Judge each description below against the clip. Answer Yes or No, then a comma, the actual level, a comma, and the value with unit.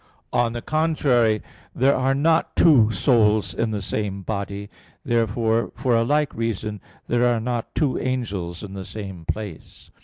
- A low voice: Yes, low, 115 Hz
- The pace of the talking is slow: No, average, 155 wpm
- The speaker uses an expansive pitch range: No, average, 3.5 semitones